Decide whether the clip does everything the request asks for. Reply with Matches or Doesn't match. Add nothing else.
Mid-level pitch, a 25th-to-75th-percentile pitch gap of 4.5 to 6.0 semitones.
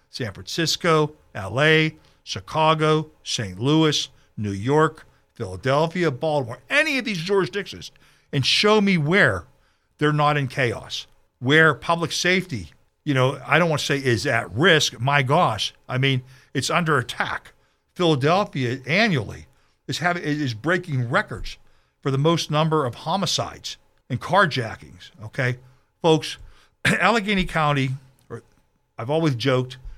Doesn't match